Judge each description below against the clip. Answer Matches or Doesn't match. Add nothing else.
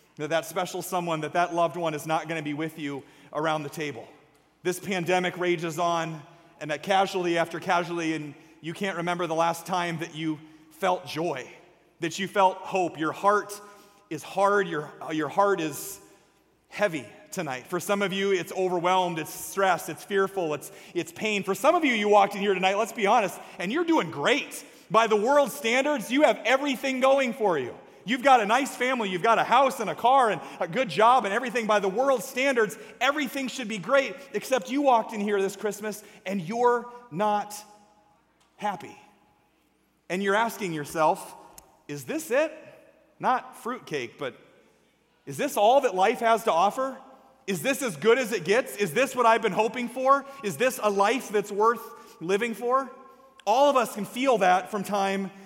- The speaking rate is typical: Matches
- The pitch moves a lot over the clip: Matches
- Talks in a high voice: Matches